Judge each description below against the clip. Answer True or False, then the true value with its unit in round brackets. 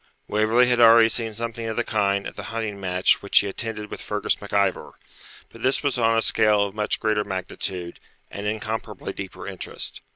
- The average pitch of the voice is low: True (105 Hz)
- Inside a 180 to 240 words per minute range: True (190 wpm)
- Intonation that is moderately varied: False (2.2 semitones)